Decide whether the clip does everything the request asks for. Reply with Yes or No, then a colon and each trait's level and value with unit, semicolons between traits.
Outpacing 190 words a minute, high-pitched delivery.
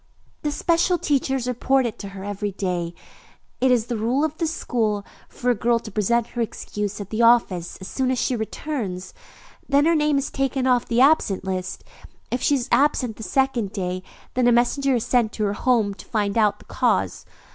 Yes: average, 200 wpm; high, 235 Hz